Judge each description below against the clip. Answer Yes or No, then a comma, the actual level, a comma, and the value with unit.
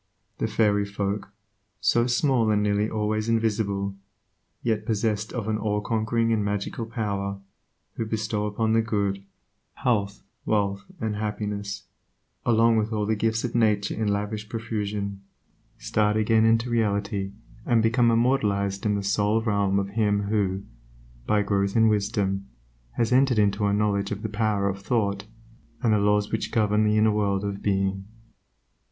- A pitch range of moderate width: No, narrow, 1.8 semitones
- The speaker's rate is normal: Yes, average, 155 wpm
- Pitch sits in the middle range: No, low, 105 Hz